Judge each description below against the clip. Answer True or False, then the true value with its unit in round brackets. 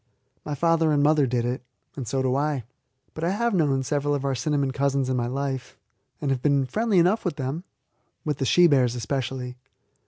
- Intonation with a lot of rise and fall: False (2.8 semitones)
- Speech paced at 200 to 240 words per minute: True (205 wpm)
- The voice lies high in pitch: False (140 Hz)